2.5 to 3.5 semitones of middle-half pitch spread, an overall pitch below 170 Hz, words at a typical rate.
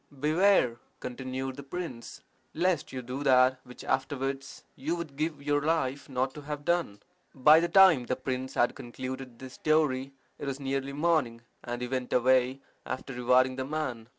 Yes: average, 2.8 semitones; low, 135 Hz; average, 170 wpm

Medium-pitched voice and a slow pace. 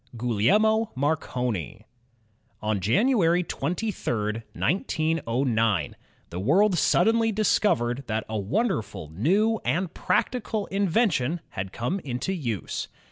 Yes: medium, 150 Hz; slow, 95 wpm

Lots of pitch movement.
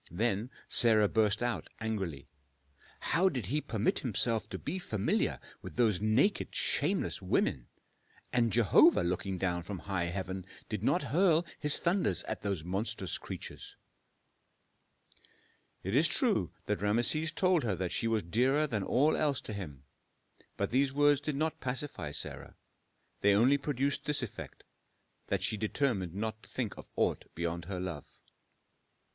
Yes: wide, 6.5 semitones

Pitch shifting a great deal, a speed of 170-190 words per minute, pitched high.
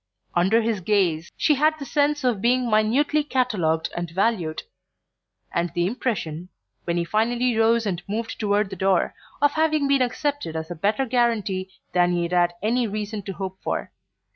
Yes: wide, 5.8 semitones; average, 175 wpm; high, 215 Hz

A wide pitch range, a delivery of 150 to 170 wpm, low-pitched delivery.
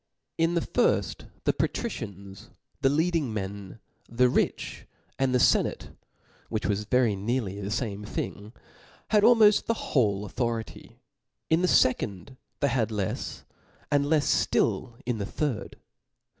No: wide, 5.9 semitones; average, 140 wpm; low, 120 Hz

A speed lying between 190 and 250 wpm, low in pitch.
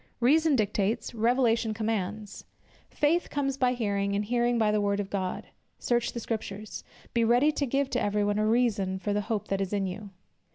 No: average, 195 wpm; high, 220 Hz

